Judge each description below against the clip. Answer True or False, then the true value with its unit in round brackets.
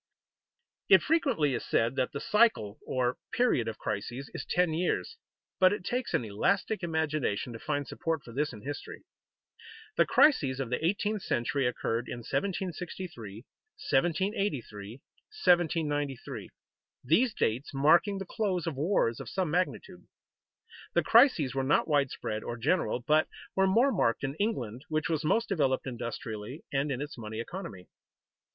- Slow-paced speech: False (150 wpm)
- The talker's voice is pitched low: False (150 Hz)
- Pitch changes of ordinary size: False (7.2 semitones)